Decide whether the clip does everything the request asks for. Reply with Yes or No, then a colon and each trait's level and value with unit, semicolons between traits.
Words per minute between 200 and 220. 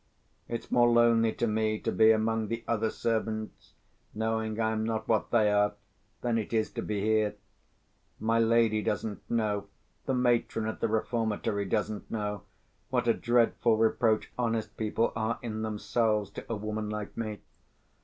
No: average, 165 wpm